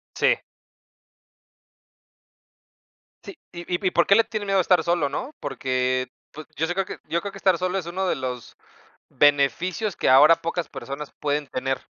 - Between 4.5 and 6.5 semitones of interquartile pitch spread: Yes, wide, 5.5 semitones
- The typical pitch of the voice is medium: Yes, medium, 170 Hz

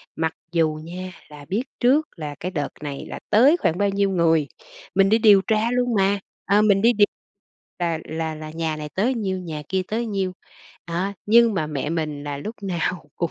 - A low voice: No, medium, 185 Hz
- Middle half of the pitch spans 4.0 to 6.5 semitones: Yes, average, 4.8 semitones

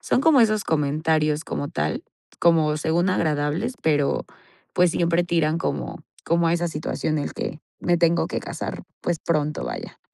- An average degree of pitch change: No, narrow, 2.2 semitones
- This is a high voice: No, medium, 165 Hz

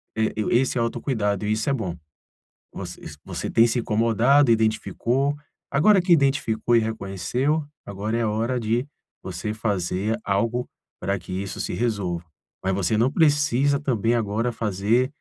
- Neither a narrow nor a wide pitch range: Yes, average, 3.6 semitones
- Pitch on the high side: No, low, 115 Hz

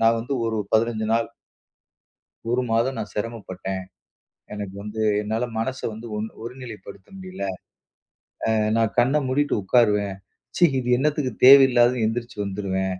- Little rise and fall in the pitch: No, average, 3.3 semitones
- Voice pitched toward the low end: Yes, low, 115 Hz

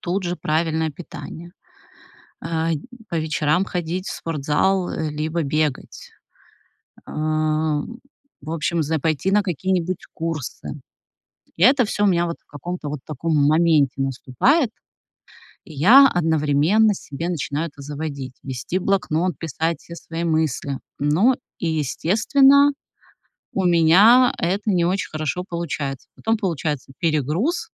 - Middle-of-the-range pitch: Yes, medium, 165 Hz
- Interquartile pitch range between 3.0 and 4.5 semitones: Yes, average, 3.4 semitones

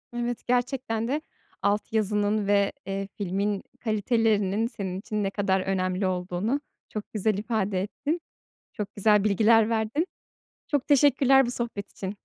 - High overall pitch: Yes, high, 210 Hz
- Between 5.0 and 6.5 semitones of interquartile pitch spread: No, average, 3.2 semitones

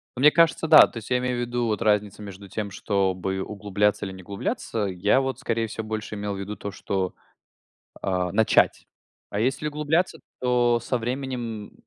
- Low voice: Yes, low, 110 Hz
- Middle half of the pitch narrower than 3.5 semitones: No, average, 3.8 semitones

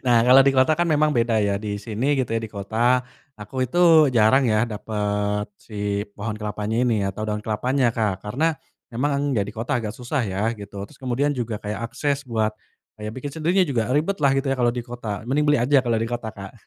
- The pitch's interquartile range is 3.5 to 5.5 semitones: Yes, average, 4.1 semitones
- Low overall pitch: Yes, low, 115 Hz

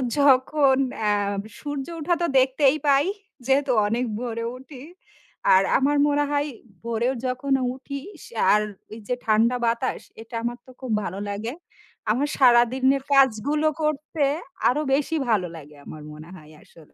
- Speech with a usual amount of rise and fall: Yes, average, 3.7 semitones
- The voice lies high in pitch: Yes, very high, 260 Hz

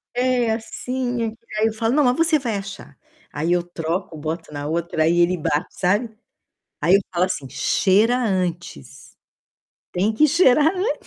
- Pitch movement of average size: No, wide, 6.2 semitones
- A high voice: Yes, high, 200 Hz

